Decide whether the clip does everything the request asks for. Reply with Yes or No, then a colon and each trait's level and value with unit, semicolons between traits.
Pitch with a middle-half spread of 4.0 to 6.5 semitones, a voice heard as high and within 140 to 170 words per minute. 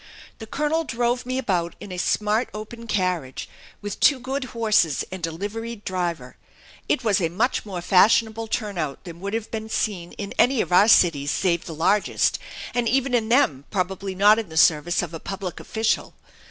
No: average, 4.7 semitones; high, 205 Hz; average, 180 wpm